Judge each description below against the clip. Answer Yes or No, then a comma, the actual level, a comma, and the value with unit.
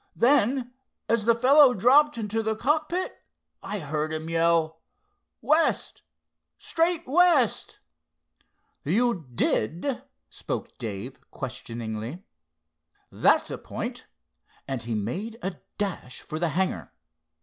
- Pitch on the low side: No, high, 205 Hz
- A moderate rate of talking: No, slow, 105 wpm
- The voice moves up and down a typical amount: No, wide, 8.6 semitones